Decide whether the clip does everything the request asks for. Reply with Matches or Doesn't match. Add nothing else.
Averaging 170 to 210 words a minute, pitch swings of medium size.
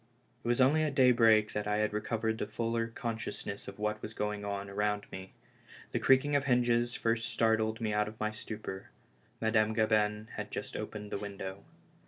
Doesn't match